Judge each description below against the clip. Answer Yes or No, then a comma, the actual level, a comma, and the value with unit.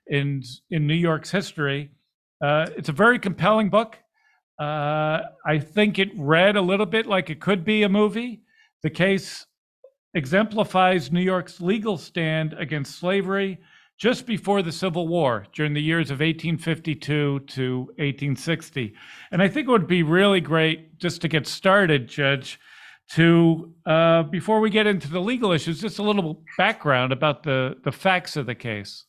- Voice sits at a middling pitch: Yes, medium, 170 Hz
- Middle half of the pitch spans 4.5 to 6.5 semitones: Yes, average, 4.8 semitones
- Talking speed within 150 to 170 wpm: Yes, average, 165 wpm